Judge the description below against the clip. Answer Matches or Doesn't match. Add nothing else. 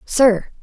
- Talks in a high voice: Matches